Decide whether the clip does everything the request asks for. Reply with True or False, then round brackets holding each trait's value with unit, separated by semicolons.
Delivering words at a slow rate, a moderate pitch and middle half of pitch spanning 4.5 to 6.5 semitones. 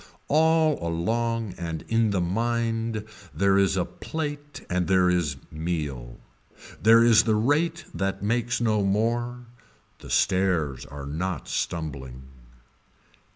False (120 wpm; 100 Hz; 5.6 semitones)